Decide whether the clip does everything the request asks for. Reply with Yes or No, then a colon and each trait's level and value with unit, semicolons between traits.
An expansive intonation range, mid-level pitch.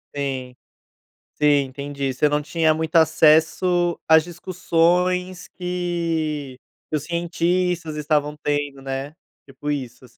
No: average, 3.2 semitones; medium, 155 Hz